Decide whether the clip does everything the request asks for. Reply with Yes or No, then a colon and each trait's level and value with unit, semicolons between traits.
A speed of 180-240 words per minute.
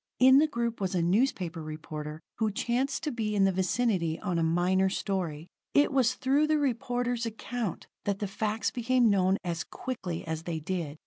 Yes: average, 185 wpm